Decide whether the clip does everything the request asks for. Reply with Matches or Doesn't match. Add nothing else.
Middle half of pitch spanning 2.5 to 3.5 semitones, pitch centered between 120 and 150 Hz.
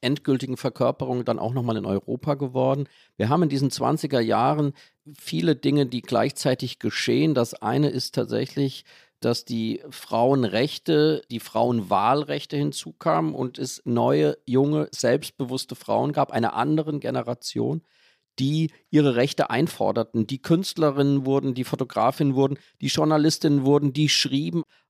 Matches